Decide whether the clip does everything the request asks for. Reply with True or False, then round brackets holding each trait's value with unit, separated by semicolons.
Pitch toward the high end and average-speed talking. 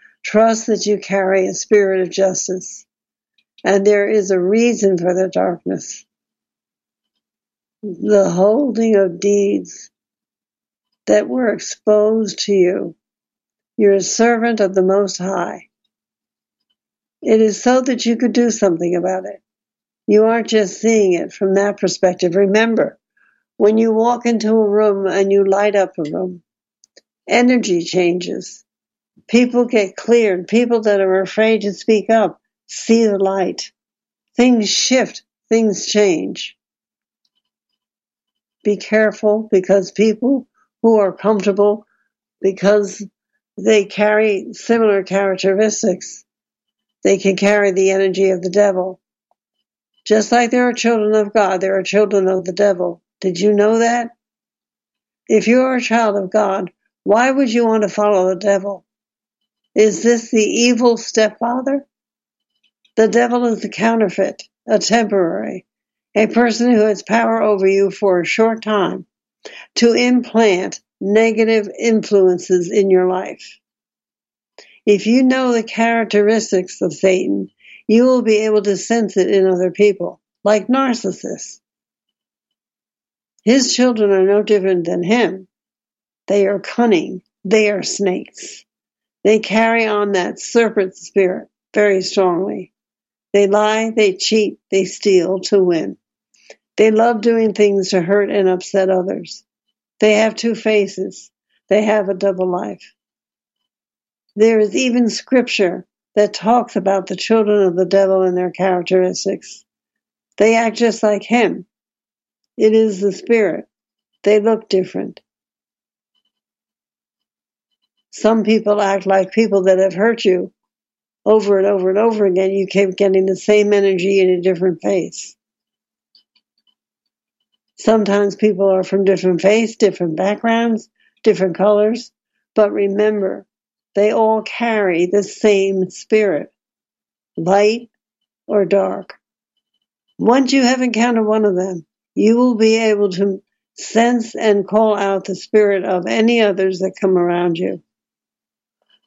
False (205 Hz; 130 wpm)